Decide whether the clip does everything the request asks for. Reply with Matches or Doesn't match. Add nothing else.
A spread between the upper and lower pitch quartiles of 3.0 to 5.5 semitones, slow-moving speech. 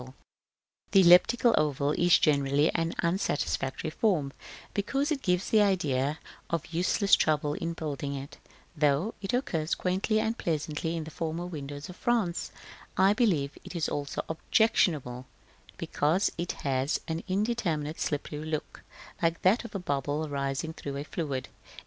Doesn't match